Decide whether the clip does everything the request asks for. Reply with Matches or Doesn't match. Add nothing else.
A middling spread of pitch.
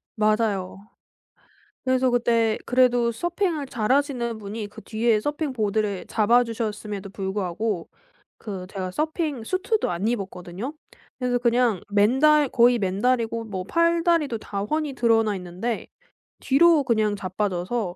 Matches